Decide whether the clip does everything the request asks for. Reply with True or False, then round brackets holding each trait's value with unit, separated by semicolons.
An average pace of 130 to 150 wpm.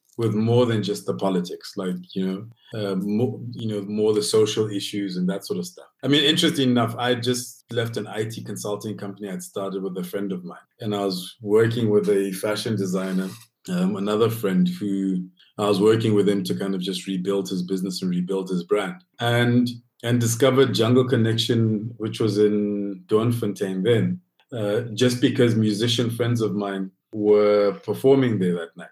False (185 wpm)